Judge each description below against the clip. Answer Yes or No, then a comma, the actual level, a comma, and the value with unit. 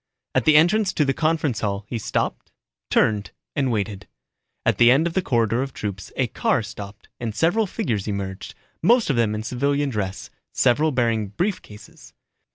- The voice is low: Yes, low, 120 Hz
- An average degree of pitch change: No, wide, 6.8 semitones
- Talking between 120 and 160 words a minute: No, average, 175 wpm